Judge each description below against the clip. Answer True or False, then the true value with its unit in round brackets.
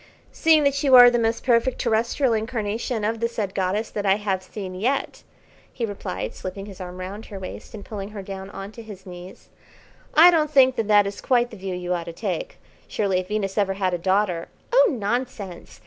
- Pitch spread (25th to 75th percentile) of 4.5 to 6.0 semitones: False (3.7 semitones)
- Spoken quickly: True (215 wpm)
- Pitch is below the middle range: False (210 Hz)